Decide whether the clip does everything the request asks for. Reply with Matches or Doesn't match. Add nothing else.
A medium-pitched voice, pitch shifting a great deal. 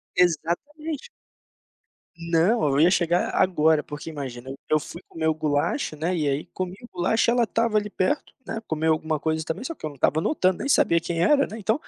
Matches